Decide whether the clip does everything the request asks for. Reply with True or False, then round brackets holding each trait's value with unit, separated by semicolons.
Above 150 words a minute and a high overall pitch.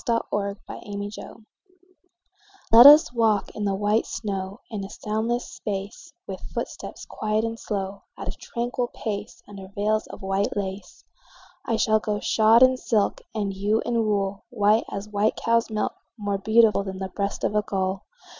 True (165 wpm; 210 Hz)